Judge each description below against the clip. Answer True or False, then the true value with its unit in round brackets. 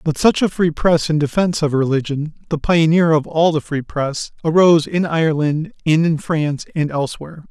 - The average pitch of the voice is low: False (155 Hz)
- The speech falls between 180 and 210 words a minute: True (190 wpm)